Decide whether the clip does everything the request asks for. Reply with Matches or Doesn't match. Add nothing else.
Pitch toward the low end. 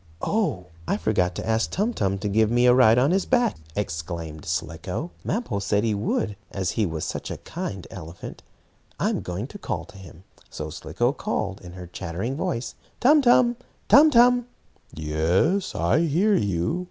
Matches